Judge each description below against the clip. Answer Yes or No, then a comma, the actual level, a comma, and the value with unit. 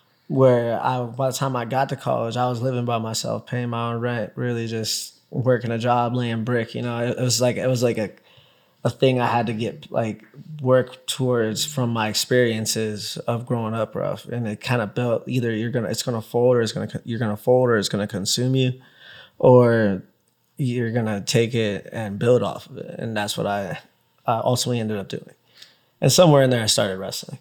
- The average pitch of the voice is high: No, low, 120 Hz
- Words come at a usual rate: No, fast, 215 wpm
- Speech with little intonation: Yes, narrow, 2.0 semitones